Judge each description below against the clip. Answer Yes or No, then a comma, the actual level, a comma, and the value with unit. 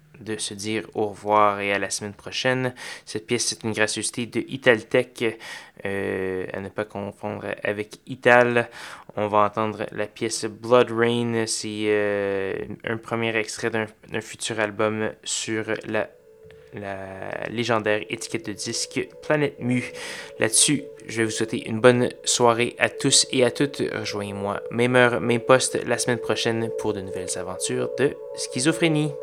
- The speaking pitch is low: Yes, low, 110 Hz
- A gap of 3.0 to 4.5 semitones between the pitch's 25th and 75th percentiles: No, narrow, 2.5 semitones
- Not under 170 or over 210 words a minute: No, average, 155 wpm